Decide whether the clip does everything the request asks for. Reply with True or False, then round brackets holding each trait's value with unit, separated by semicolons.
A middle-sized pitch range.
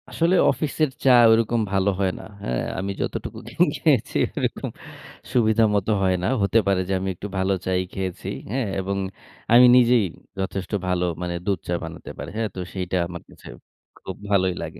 True (3.4 semitones)